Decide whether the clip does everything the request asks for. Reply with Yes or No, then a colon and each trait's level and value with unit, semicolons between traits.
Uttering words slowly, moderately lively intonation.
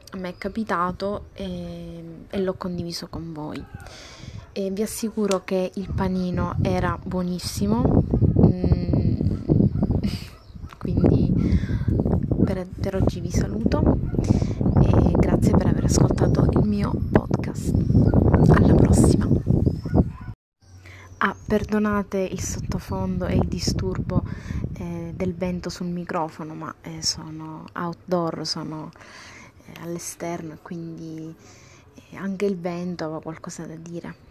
Yes: slow, 100 wpm; average, 3.4 semitones